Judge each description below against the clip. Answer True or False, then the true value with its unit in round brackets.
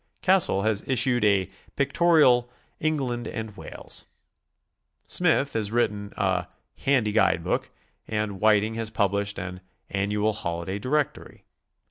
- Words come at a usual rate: False (110 wpm)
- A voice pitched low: True (110 Hz)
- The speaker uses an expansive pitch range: False (3.8 semitones)